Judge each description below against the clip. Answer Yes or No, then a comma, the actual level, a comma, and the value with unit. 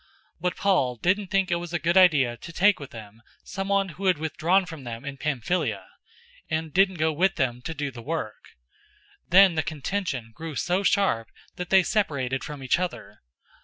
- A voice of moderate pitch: Yes, medium, 160 Hz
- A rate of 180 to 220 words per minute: Yes, average, 200 wpm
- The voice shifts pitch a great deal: Yes, wide, 5.9 semitones